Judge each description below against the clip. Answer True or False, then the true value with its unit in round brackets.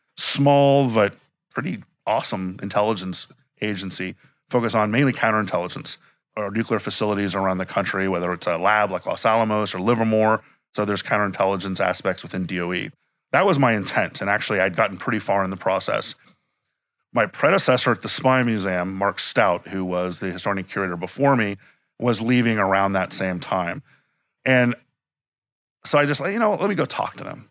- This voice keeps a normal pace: True (170 wpm)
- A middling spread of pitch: True (4.3 semitones)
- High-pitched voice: False (105 Hz)